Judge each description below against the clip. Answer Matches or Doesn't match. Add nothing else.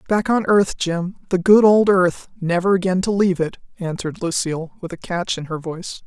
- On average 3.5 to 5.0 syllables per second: Doesn't match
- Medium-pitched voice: Matches